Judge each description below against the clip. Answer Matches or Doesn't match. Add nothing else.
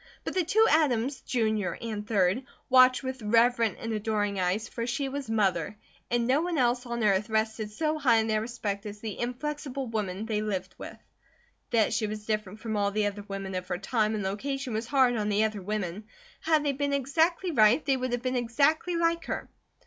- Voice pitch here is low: Doesn't match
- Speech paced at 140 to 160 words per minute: Doesn't match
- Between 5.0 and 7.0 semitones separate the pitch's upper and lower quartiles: Doesn't match